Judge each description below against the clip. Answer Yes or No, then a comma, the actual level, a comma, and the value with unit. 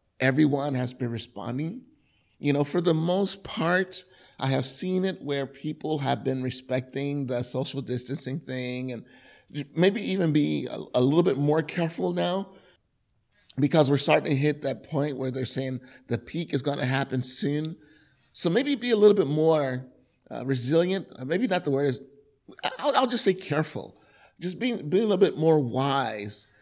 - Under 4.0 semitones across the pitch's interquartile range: No, average, 4.7 semitones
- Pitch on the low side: No, medium, 145 Hz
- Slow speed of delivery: No, average, 175 wpm